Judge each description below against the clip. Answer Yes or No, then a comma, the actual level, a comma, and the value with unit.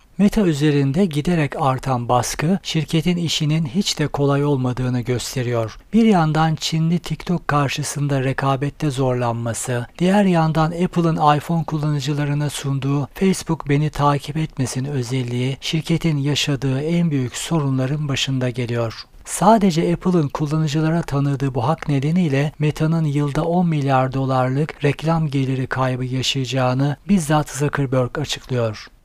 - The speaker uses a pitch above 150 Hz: No, medium, 145 Hz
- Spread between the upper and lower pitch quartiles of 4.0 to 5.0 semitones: No, average, 3.4 semitones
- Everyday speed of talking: Yes, average, 115 wpm